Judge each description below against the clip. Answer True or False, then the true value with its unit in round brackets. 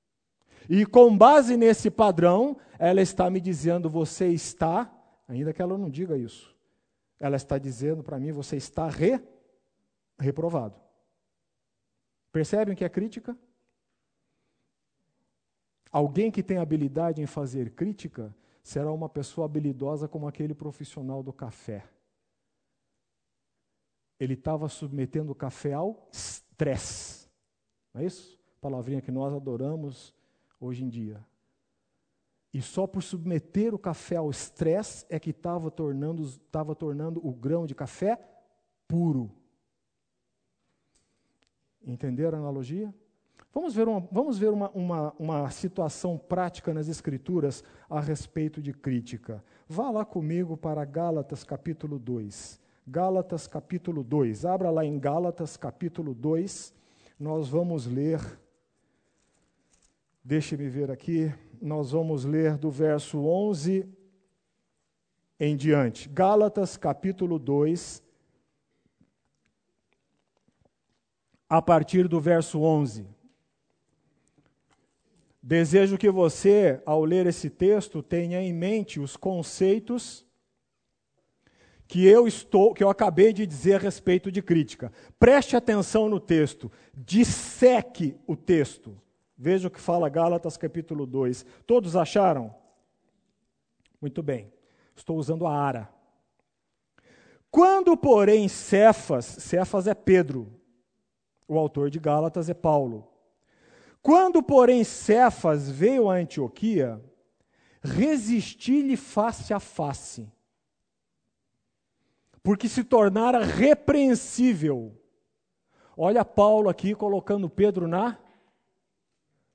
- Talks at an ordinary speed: False (110 wpm)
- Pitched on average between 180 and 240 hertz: False (165 Hz)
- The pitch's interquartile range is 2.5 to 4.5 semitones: False (5.3 semitones)